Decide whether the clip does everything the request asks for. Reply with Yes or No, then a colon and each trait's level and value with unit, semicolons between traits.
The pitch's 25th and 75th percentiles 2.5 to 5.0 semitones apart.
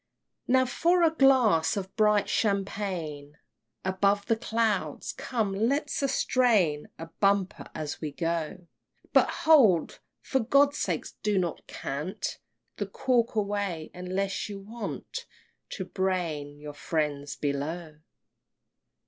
No: wide, 5.6 semitones